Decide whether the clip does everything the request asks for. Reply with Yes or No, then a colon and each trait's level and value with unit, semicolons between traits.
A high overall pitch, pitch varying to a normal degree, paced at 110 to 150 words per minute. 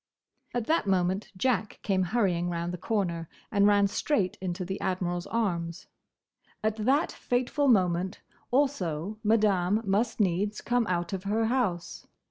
Yes: high, 200 Hz; average, 4.0 semitones; average, 140 wpm